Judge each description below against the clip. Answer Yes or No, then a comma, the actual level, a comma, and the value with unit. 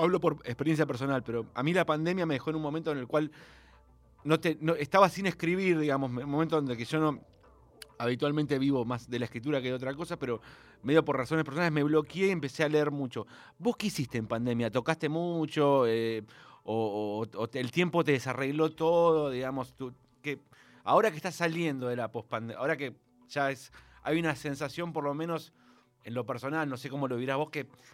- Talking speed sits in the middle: No, fast, 215 wpm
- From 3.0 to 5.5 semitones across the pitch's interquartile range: Yes, average, 4.4 semitones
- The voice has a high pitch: No, medium, 145 Hz